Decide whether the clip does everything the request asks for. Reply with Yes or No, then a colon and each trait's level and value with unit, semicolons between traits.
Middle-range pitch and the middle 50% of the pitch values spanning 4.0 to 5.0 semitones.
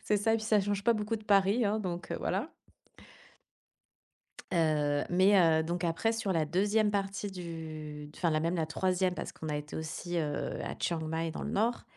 Yes: medium, 180 Hz; average, 4.3 semitones